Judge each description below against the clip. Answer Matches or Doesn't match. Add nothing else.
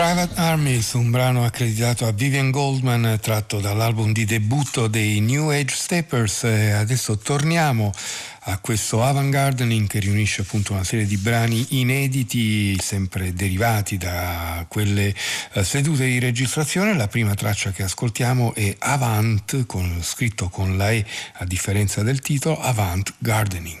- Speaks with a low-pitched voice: Matches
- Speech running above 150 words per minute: Doesn't match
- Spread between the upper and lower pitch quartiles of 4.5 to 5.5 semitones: Doesn't match